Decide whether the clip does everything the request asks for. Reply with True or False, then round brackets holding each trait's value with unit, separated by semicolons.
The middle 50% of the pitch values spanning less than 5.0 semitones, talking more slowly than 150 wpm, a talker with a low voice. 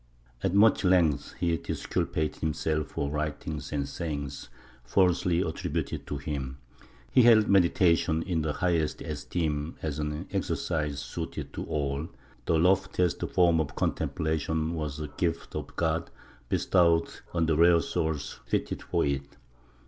True (2.5 semitones; 140 wpm; 80 Hz)